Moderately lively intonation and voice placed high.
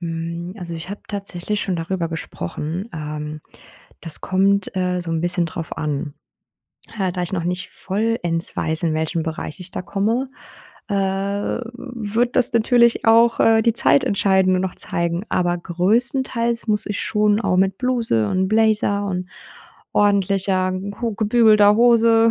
Yes: average, 4.3 semitones; high, 195 Hz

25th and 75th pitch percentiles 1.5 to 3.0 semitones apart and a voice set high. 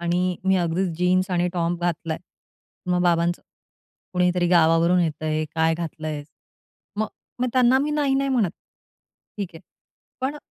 No: narrow, 2.5 semitones; medium, 175 Hz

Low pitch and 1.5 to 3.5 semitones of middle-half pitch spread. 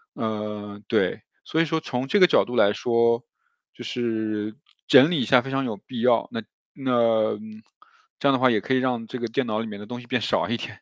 Yes: low, 120 Hz; average, 3.0 semitones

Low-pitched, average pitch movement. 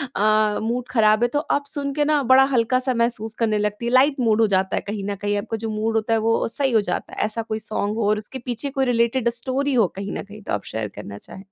No: high, 225 Hz; average, 3.0 semitones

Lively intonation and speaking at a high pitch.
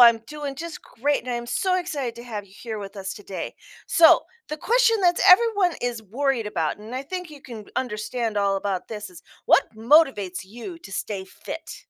Yes: wide, 6.5 semitones; high, 240 Hz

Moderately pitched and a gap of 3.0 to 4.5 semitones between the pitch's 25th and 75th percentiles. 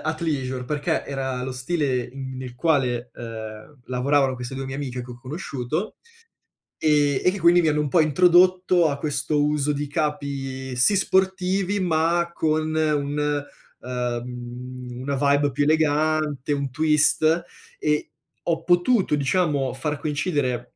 Yes: medium, 145 Hz; average, 3.3 semitones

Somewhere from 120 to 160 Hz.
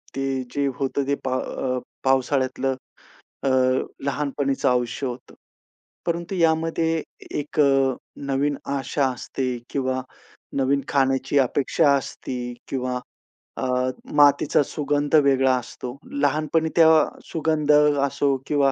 Yes: medium, 140 Hz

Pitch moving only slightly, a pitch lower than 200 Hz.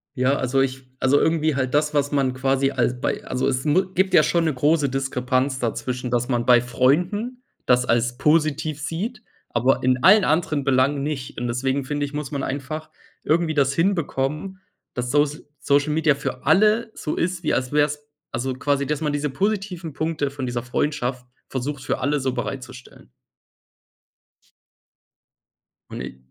No: average, 3.2 semitones; medium, 140 Hz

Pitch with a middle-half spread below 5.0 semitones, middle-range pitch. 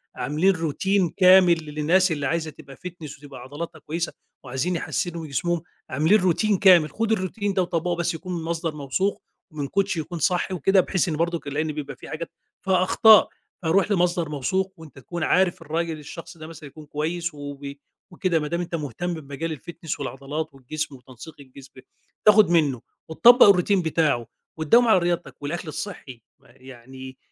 Yes: average, 3.7 semitones; medium, 165 Hz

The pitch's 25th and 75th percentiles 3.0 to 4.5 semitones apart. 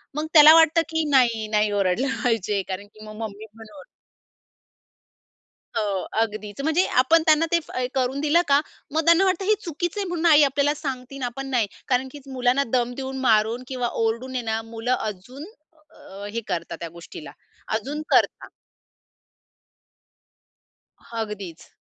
No: wide, 5.5 semitones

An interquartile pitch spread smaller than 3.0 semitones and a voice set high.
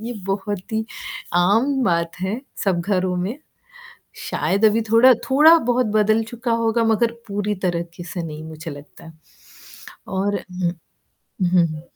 No: average, 4.6 semitones; high, 200 Hz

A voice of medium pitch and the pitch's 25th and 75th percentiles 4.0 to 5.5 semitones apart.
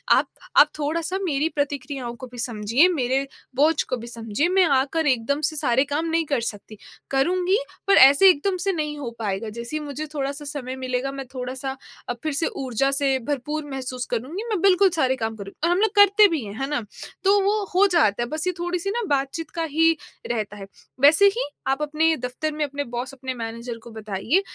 No: very high, 280 Hz; average, 4.6 semitones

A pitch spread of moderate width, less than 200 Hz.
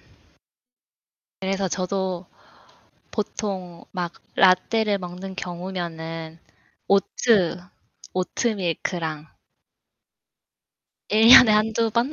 Yes: average, 3.3 semitones; high, 190 Hz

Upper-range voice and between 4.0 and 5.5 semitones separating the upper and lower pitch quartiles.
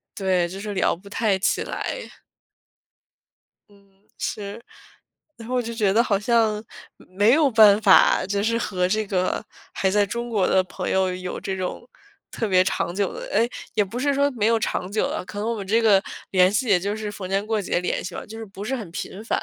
No: high, 205 Hz; average, 2.8 semitones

